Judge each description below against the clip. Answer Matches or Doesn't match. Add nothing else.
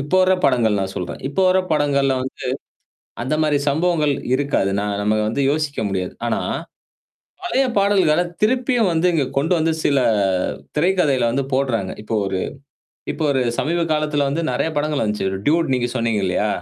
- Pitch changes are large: Matches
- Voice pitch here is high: Doesn't match